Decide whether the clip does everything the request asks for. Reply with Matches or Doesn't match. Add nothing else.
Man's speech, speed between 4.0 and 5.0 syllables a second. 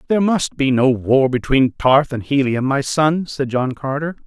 Matches